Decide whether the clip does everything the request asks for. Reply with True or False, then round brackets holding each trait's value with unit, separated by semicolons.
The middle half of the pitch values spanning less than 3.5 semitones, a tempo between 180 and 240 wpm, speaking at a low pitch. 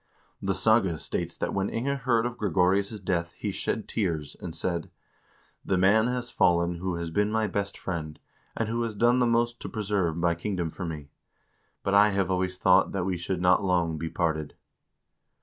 False (4.1 semitones; 195 wpm; 95 Hz)